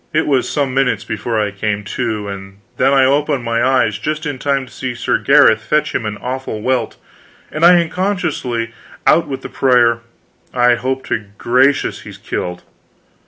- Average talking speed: Yes, average, 175 wpm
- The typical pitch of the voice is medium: No, low, 125 Hz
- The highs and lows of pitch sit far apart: No, average, 3.5 semitones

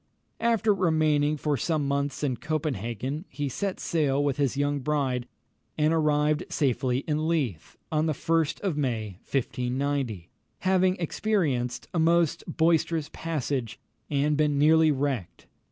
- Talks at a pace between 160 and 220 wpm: No, slow, 135 wpm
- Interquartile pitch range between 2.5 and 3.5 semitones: Yes, average, 3.1 semitones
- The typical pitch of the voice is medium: Yes, medium, 145 Hz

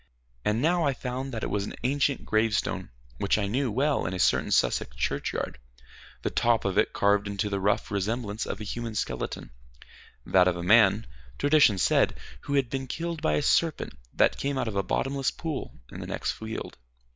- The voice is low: Yes, low, 115 Hz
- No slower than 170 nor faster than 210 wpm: Yes, average, 195 wpm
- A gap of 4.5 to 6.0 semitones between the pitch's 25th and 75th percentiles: Yes, average, 5.2 semitones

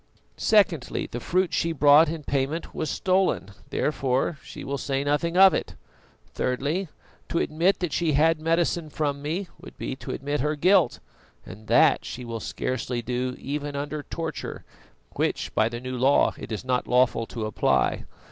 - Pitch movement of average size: Yes, average, 4.5 semitones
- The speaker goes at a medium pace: Yes, average, 165 wpm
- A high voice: No, medium, 145 Hz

